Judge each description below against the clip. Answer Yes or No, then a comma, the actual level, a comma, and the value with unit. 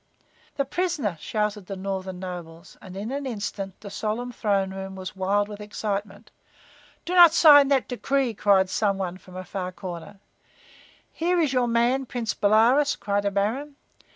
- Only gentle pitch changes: No, average, 4.8 semitones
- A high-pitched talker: Yes, high, 205 Hz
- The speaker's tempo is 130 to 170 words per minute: Yes, average, 165 wpm